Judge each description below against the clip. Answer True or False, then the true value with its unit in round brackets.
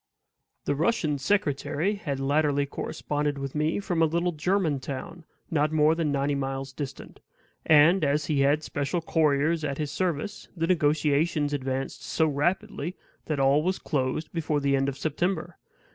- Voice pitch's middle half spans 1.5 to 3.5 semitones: True (2.8 semitones)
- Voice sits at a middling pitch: True (150 Hz)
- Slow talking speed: False (160 wpm)